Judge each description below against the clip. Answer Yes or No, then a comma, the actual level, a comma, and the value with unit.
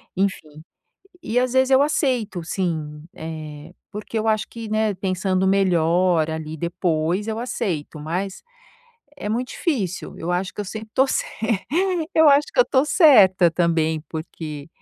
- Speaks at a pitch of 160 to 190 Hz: Yes, medium, 185 Hz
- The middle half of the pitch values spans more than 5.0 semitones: Yes, wide, 5.4 semitones